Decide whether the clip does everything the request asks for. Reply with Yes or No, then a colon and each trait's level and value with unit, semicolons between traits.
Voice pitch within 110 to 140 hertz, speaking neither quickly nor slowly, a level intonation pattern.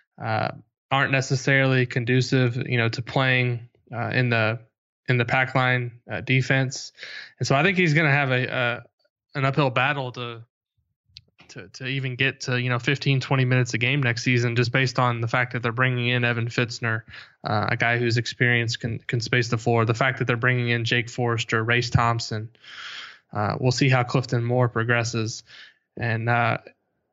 Yes: low, 125 Hz; average, 190 wpm; narrow, 1.8 semitones